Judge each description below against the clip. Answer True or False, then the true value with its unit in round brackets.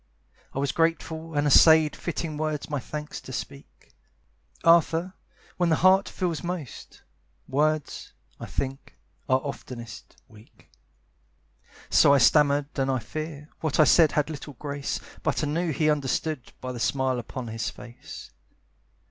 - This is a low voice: False (150 Hz)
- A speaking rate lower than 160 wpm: True (145 wpm)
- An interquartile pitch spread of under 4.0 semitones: True (3.2 semitones)